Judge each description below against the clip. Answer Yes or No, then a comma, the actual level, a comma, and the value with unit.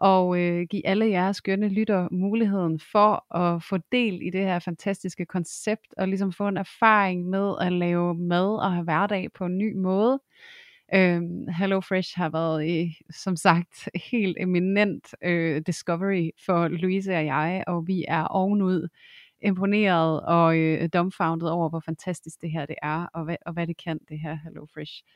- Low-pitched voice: No, medium, 180 Hz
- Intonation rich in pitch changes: No, average, 2.8 semitones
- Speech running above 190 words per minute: No, average, 175 wpm